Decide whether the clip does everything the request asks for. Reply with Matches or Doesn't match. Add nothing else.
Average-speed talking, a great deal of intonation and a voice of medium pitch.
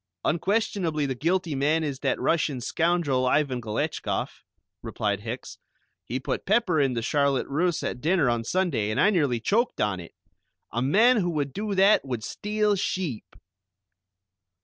Matches